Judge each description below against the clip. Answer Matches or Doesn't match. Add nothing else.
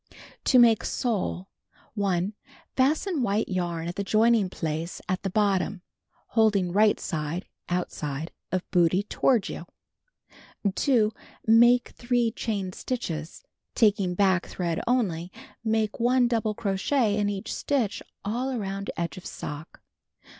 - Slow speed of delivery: Matches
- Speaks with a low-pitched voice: Doesn't match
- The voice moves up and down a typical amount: Matches